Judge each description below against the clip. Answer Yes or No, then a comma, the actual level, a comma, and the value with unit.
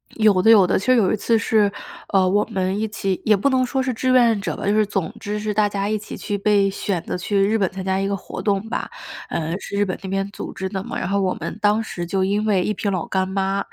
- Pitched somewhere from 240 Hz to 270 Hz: No, high, 200 Hz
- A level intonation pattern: Yes, narrow, 2.0 semitones